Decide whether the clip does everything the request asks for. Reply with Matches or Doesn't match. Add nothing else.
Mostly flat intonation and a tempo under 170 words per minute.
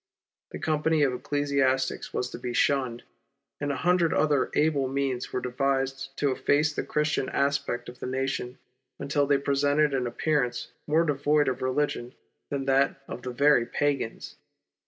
Matches